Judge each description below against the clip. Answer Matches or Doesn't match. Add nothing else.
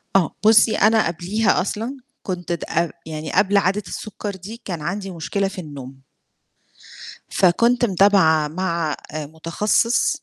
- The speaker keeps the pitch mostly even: Doesn't match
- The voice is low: Doesn't match